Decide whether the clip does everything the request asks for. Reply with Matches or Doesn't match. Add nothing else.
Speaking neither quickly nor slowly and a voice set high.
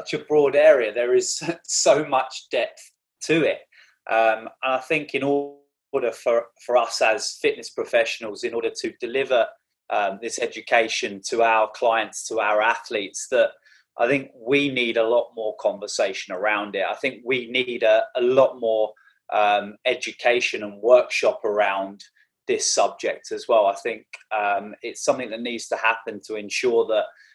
Doesn't match